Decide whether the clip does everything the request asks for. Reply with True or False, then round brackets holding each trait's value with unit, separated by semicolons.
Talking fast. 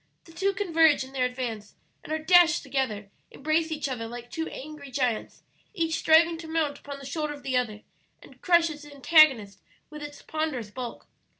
False (185 wpm)